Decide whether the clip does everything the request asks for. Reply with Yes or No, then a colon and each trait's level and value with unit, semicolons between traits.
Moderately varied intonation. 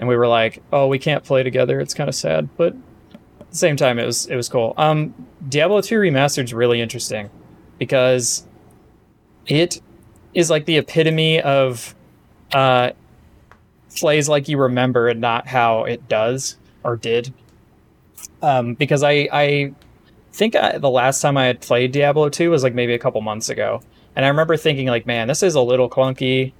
Yes: average, 3.7 semitones